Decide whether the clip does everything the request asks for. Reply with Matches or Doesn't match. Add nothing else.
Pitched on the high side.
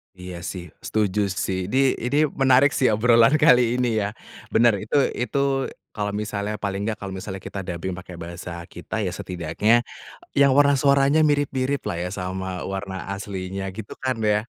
Doesn't match